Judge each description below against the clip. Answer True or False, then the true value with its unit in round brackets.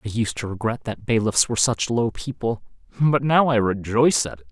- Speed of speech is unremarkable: False (215 wpm)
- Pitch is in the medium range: False (115 Hz)